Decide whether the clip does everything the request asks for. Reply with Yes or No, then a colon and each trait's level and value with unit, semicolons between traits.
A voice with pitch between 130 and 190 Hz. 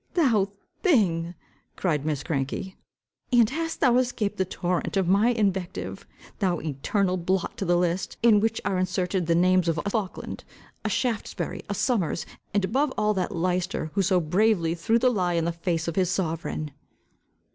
Yes: medium, 185 Hz